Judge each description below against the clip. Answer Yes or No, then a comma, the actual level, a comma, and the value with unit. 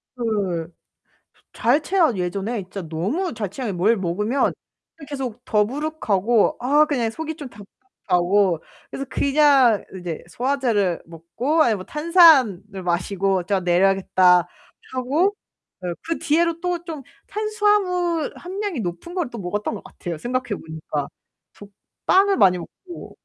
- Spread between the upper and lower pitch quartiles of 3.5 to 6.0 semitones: No, wide, 8.5 semitones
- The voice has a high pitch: Yes, high, 235 Hz